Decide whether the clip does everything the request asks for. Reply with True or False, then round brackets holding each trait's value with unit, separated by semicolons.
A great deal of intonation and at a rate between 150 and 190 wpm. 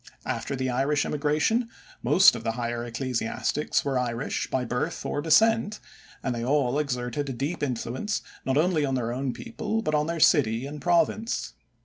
False (3.8 semitones; 170 wpm)